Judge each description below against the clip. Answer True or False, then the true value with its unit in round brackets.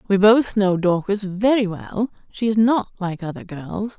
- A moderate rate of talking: True (180 wpm)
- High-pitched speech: True (200 Hz)